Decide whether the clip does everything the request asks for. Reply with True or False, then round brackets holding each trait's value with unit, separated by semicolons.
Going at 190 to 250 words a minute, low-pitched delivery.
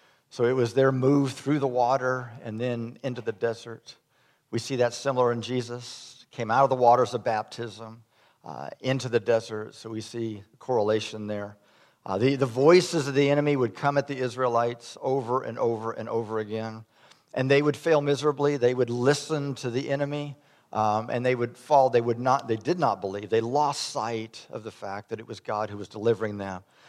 True (200 wpm; 120 Hz)